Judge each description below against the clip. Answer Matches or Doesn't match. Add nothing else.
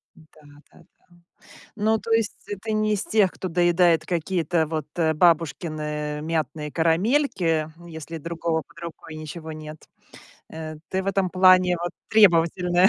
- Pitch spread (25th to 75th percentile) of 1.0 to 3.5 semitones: Matches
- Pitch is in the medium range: Matches